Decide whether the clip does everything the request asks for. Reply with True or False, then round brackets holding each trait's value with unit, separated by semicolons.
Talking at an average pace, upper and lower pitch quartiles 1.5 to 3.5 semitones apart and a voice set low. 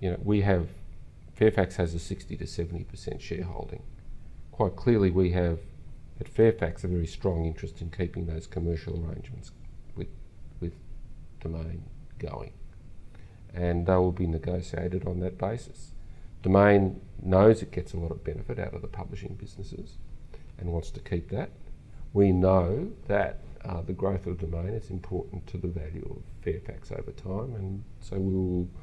True (160 wpm; 2.8 semitones; 90 Hz)